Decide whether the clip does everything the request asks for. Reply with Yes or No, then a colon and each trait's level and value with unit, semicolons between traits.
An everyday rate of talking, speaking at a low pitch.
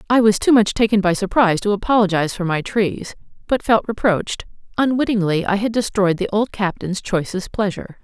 No: average, 180 wpm; high, 205 Hz